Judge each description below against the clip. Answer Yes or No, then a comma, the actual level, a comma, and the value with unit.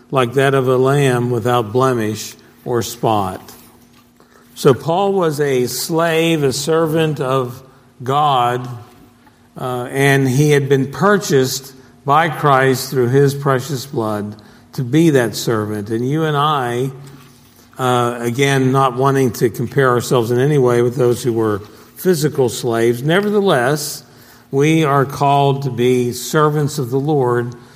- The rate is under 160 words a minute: Yes, average, 140 wpm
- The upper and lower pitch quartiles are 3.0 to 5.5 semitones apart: No, narrow, 2.6 semitones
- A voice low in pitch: Yes, low, 130 Hz